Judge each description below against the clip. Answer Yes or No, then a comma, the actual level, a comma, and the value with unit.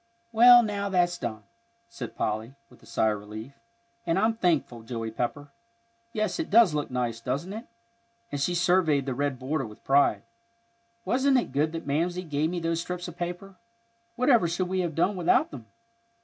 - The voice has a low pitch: No, medium, 165 Hz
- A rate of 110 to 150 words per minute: No, average, 180 wpm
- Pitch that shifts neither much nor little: No, wide, 6.0 semitones